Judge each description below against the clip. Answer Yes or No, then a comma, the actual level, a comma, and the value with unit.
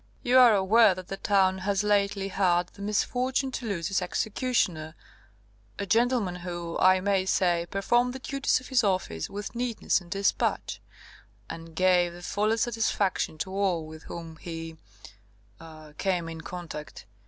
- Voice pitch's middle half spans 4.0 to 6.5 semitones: No, average, 3.6 semitones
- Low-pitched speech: No, high, 190 Hz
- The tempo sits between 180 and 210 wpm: No, average, 155 wpm